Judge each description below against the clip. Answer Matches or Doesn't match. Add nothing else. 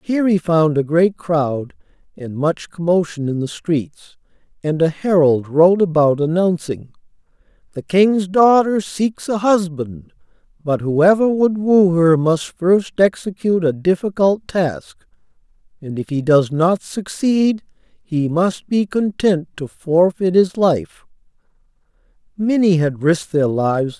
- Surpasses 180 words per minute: Doesn't match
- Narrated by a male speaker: Matches